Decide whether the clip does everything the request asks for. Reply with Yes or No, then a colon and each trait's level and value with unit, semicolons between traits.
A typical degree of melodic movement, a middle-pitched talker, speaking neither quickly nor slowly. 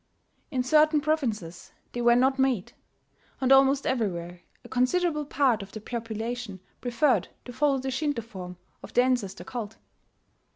No: average, 3.7 semitones; high, 245 Hz; average, 150 wpm